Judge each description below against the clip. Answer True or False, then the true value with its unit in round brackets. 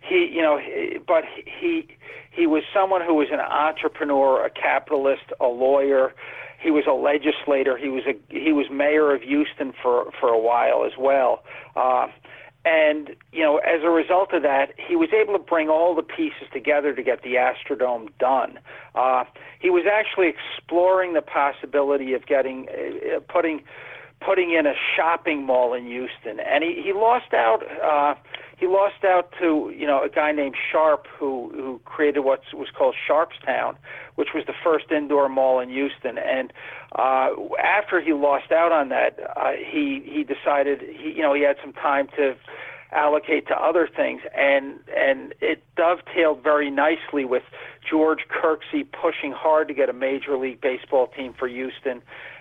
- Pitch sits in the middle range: True (155 Hz)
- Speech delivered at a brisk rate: False (170 wpm)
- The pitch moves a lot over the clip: True (6.5 semitones)